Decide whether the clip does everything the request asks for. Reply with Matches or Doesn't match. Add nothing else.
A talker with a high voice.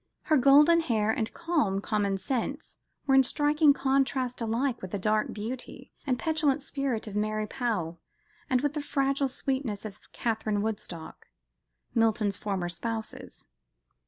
Matches